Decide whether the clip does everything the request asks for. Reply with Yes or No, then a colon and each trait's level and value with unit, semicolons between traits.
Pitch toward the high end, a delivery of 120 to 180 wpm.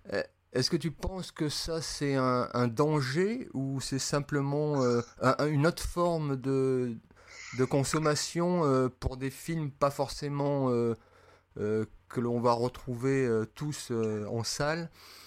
No: low, 135 Hz; average, 150 wpm